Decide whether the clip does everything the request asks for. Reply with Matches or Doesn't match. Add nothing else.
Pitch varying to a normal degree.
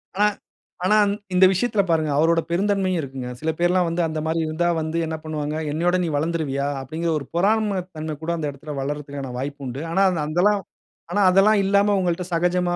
Matches